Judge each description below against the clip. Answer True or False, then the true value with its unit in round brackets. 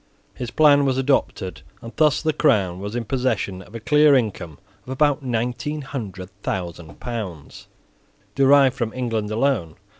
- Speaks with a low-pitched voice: True (120 Hz)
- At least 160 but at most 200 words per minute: False (150 wpm)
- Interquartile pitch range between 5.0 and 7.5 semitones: True (5.5 semitones)